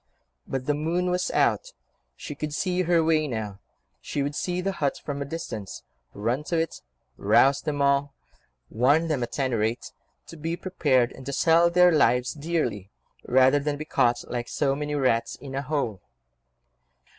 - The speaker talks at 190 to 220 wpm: No, average, 175 wpm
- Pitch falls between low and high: Yes, medium, 145 Hz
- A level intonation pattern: No, average, 4.1 semitones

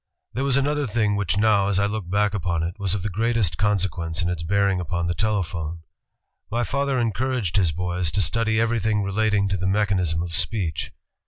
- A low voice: Yes, low, 100 Hz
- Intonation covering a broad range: No, average, 3.9 semitones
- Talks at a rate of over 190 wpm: Yes, average, 200 wpm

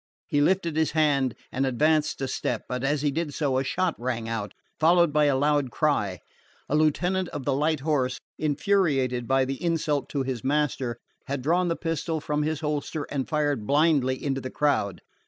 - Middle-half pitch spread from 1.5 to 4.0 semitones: Yes, average, 2.9 semitones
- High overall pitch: No, medium, 145 Hz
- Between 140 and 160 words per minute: No, average, 190 wpm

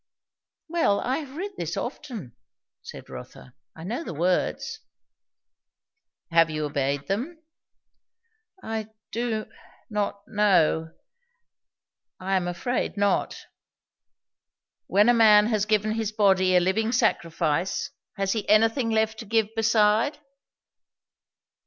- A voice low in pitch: No, high, 210 Hz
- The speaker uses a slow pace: Yes, slow, 115 wpm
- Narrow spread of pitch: No, average, 3.6 semitones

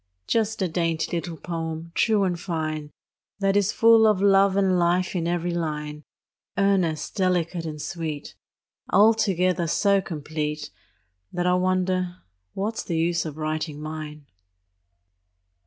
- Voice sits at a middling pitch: Yes, medium, 175 Hz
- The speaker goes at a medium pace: No, slow, 130 wpm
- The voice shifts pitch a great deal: No, average, 3.4 semitones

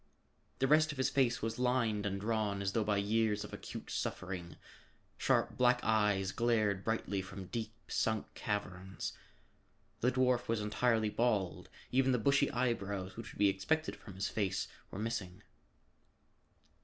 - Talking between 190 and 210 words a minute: No, average, 155 wpm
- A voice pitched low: Yes, low, 110 Hz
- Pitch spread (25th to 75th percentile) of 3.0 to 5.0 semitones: Yes, average, 3.5 semitones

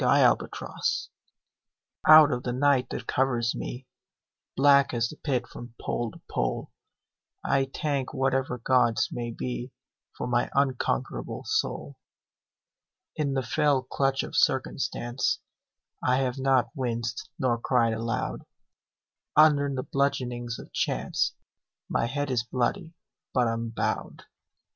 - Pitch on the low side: Yes, low, 130 Hz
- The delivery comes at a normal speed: No, slow, 125 wpm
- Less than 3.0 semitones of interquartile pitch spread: Yes, narrow, 2.4 semitones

